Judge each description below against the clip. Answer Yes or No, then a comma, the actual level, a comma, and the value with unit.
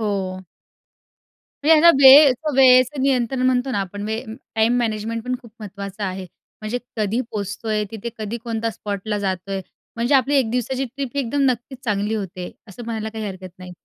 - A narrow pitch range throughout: No, average, 3.7 semitones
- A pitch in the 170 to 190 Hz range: No, high, 225 Hz